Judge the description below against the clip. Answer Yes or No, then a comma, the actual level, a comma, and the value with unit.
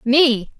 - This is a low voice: No, very high, 255 Hz